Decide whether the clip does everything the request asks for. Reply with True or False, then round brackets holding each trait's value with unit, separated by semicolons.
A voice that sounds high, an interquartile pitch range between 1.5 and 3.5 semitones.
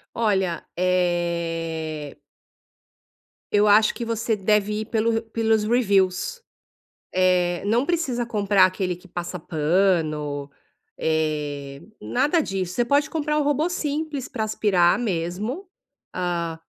False (195 Hz; 5.2 semitones)